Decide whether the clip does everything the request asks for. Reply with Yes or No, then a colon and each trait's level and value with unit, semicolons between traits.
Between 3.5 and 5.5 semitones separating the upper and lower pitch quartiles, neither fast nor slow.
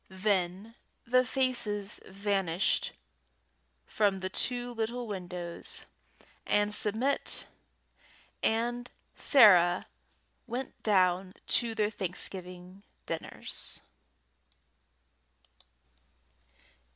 No: average, 4.0 semitones; slow, 65 wpm